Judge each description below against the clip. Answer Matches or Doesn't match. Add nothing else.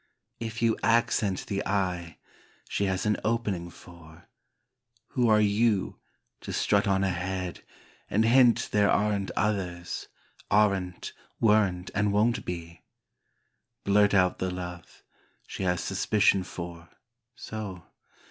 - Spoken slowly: Matches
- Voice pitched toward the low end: Matches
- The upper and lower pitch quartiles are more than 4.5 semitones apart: Doesn't match